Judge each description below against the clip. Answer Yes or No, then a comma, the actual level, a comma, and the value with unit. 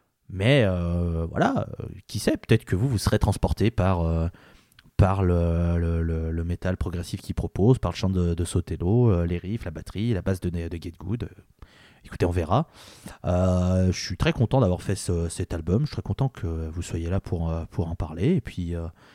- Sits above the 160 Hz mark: No, very low, 90 Hz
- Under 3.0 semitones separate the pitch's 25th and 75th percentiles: No, average, 3.4 semitones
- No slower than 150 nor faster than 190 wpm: No, average, 210 wpm